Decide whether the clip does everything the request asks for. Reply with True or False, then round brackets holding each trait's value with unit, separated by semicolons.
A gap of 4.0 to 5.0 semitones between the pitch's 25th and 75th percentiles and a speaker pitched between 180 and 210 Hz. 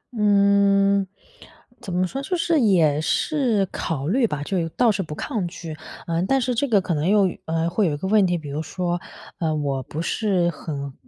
True (4.5 semitones; 185 Hz)